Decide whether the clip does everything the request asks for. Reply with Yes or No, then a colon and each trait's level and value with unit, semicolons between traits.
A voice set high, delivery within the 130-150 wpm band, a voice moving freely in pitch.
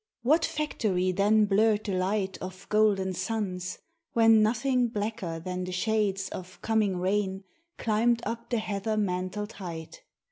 No: high, 205 Hz; average, 140 wpm; average, 3.1 semitones